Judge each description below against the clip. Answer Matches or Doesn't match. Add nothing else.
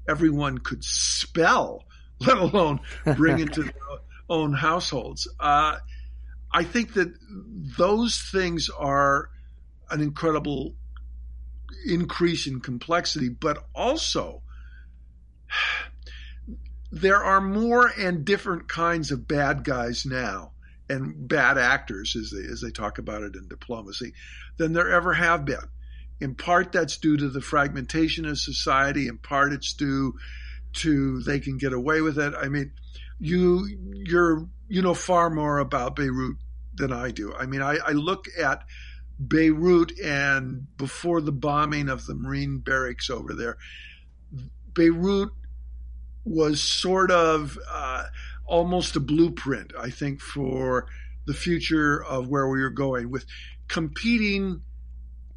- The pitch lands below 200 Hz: Matches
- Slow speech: Matches